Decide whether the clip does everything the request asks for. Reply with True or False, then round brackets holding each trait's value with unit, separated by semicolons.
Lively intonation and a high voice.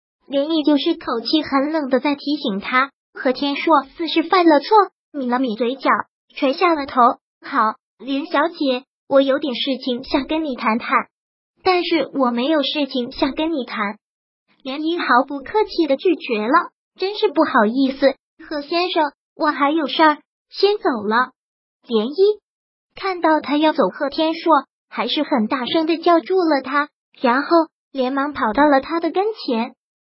False (3.8 semitones; 290 Hz)